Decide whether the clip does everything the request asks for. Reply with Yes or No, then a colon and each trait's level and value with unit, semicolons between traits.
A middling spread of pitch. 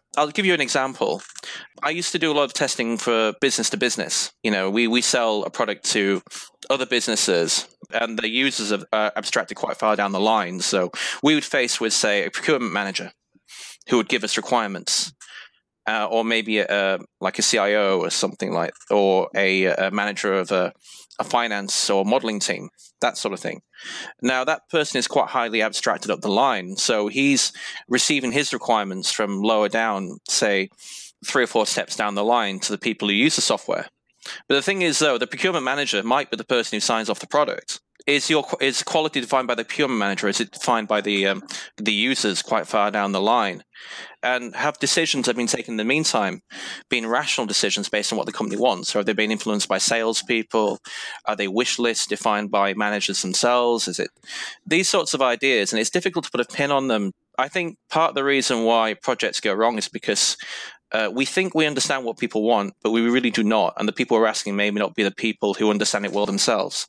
Yes: average, 4.1 semitones